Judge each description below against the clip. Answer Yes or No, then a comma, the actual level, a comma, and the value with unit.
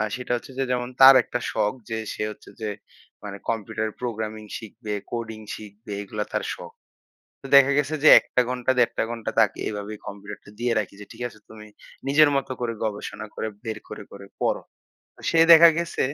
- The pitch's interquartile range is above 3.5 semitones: No, average, 2.9 semitones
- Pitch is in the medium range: No, low, 110 Hz